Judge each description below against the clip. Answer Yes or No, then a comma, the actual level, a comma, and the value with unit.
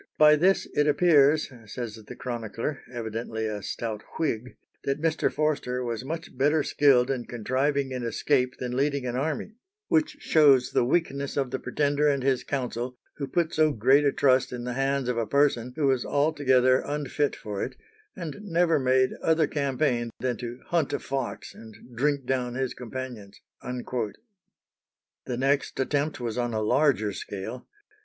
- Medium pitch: No, low, 130 Hz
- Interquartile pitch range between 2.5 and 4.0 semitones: Yes, average, 3.2 semitones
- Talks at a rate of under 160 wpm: No, average, 165 wpm